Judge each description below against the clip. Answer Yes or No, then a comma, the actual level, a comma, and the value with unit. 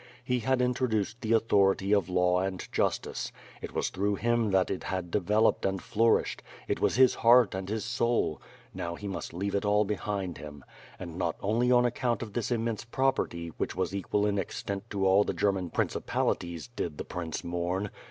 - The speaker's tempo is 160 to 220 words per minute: Yes, average, 190 wpm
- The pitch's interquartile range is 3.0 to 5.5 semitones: Yes, average, 3.8 semitones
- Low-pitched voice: Yes, low, 100 Hz